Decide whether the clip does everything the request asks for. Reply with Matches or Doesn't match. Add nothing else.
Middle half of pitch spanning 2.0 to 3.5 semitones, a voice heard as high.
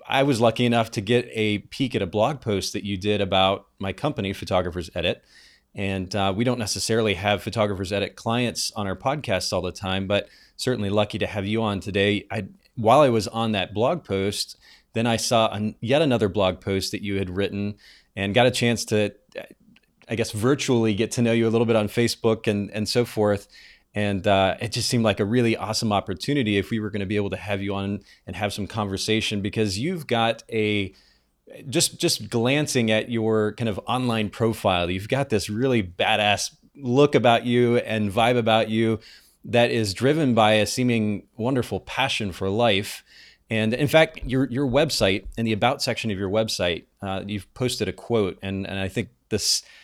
Doesn't match